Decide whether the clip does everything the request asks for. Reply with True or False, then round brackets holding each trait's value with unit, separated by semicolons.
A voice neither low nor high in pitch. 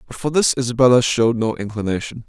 False (120 Hz)